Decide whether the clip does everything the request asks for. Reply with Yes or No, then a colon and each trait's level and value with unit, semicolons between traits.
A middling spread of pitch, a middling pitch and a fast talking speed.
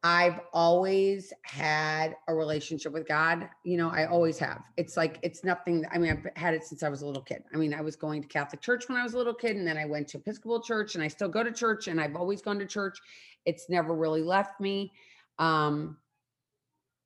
Yes: average, 4.0 semitones; medium, 165 Hz; fast, 230 wpm